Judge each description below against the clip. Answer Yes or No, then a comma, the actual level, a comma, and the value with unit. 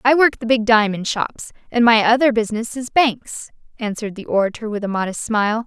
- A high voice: Yes, high, 225 Hz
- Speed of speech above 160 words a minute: Yes, average, 200 wpm